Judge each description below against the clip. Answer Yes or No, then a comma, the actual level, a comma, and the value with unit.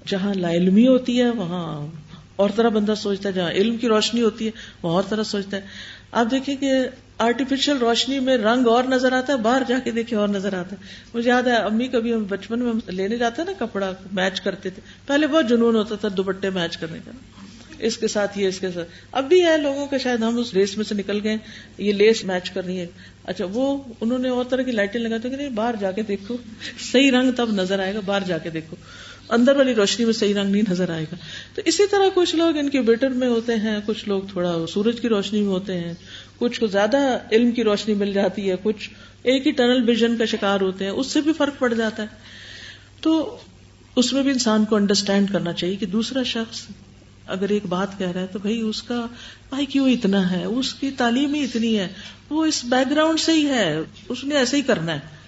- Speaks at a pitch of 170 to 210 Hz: No, high, 220 Hz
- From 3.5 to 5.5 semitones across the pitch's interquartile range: Yes, average, 4.3 semitones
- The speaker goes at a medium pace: No, fast, 235 wpm